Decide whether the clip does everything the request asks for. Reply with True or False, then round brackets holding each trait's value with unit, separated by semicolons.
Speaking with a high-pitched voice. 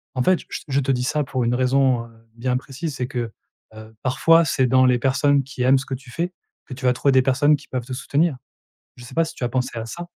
False (130 Hz)